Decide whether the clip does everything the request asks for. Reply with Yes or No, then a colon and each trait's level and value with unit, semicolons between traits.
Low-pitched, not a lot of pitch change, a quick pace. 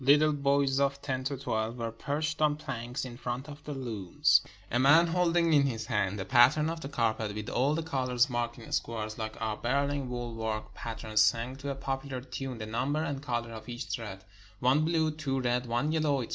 No: low, 130 Hz; average, 3.8 semitones; fast, 215 wpm